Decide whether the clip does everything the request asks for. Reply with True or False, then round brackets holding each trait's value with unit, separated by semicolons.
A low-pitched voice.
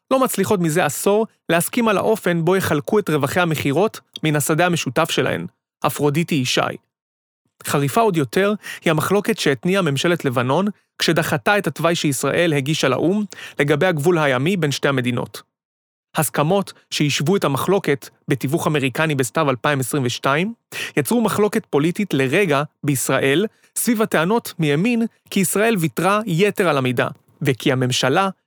False (165 Hz)